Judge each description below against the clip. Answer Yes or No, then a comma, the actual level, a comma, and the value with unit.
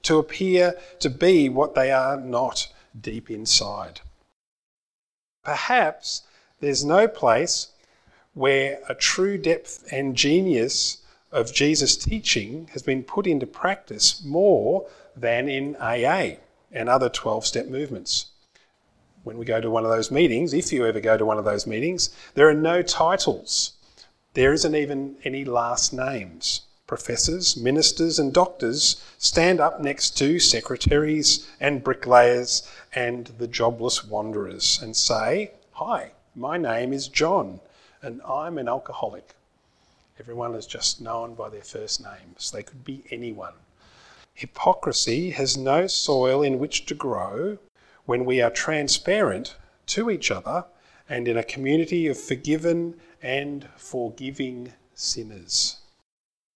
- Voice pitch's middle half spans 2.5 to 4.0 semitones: No, average, 4.7 semitones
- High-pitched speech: No, low, 135 Hz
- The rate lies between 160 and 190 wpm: No, slow, 135 wpm